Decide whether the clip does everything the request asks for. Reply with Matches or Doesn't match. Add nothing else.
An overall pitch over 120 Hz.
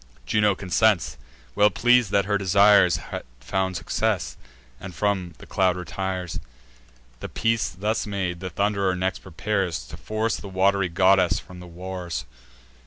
Doesn't match